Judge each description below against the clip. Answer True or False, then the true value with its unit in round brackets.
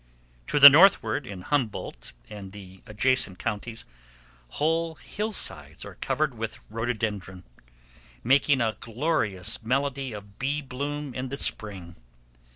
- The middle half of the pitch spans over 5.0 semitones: True (5.6 semitones)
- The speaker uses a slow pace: True (120 wpm)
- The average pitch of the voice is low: True (120 Hz)